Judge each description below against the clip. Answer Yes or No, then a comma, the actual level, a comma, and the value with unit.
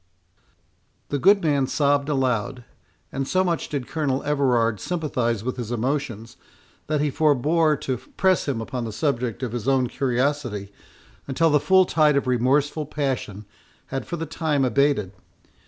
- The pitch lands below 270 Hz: Yes, low, 135 Hz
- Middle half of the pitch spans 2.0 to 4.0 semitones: Yes, average, 3.6 semitones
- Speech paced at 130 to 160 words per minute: Yes, average, 155 wpm